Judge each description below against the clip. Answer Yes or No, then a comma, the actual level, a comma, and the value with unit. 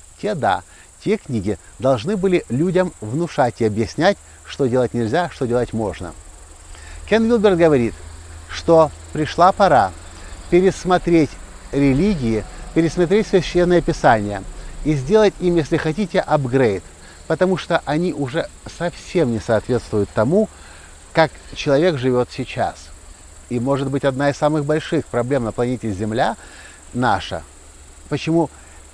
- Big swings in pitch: Yes, wide, 9.0 semitones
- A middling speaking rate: Yes, average, 120 wpm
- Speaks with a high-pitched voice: No, low, 135 Hz